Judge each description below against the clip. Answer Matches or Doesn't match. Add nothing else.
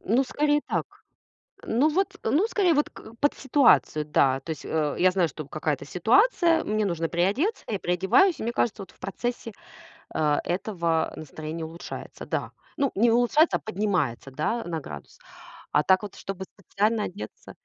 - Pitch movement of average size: Doesn't match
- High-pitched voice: Matches